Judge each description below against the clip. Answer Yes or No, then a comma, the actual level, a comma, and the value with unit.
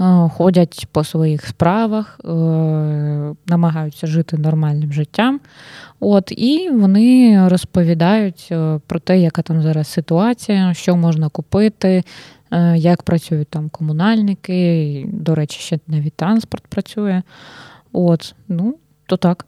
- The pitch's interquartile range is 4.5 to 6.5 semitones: No, average, 3.7 semitones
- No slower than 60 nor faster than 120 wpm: Yes, average, 110 wpm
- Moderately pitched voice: Yes, medium, 170 Hz